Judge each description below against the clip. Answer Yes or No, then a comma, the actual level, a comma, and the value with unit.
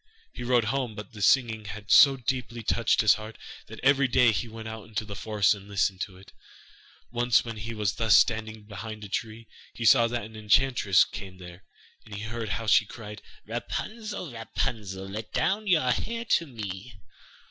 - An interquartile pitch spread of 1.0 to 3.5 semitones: Yes, average, 2.7 semitones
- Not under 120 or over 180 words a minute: No, average, 190 wpm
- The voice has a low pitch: Yes, low, 110 Hz